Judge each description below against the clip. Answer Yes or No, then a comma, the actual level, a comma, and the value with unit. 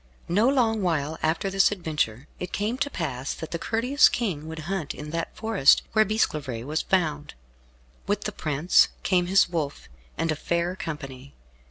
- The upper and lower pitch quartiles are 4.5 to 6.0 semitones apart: Yes, average, 5.1 semitones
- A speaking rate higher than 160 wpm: Yes, average, 170 wpm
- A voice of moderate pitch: Yes, medium, 165 Hz